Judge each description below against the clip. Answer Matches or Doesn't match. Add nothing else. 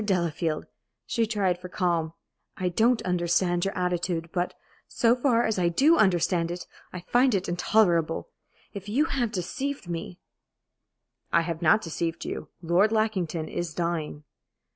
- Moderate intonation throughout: Matches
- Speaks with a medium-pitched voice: Matches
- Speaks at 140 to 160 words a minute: Matches